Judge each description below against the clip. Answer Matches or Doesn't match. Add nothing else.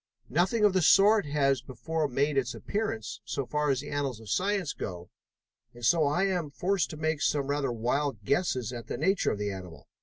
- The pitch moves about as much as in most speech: Doesn't match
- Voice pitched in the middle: Matches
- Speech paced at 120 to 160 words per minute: Doesn't match